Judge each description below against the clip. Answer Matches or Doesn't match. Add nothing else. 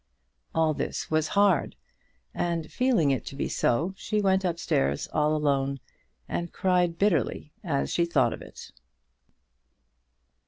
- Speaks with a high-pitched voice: Doesn't match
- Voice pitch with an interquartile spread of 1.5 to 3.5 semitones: Doesn't match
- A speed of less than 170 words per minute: Matches